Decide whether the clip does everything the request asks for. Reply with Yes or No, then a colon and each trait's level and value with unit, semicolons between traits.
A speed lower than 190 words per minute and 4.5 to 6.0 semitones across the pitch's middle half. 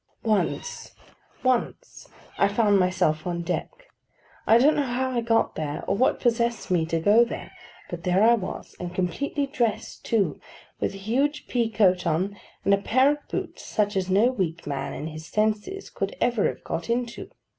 Yes: average, 175 wpm; average, 5.0 semitones